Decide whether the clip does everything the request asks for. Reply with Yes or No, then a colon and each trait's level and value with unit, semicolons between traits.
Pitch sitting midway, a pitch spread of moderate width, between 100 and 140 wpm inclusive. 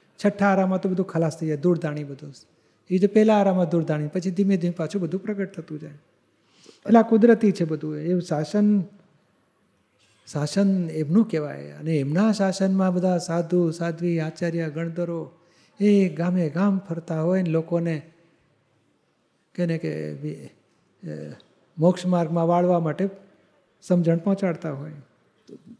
Yes: medium, 170 Hz; average, 3.4 semitones; average, 135 wpm